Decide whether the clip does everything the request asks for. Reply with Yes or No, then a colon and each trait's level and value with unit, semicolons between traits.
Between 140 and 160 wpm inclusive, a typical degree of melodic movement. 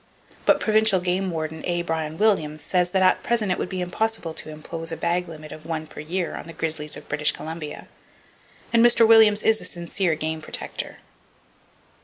No: average, 190 wpm; average, 3.5 semitones